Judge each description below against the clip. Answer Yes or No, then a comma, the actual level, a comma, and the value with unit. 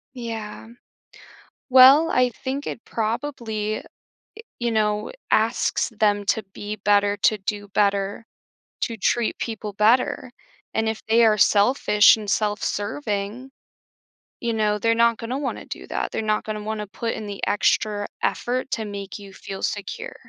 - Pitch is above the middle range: Yes, high, 215 Hz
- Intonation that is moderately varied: No, narrow, 2.1 semitones